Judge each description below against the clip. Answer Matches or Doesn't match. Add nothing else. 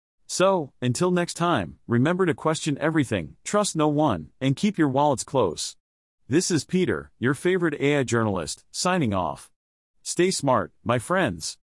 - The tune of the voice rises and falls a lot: Matches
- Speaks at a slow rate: Doesn't match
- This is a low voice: Doesn't match